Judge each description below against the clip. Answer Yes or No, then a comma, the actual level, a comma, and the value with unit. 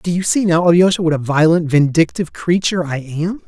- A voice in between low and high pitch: Yes, medium, 170 Hz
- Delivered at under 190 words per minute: No, fast, 205 wpm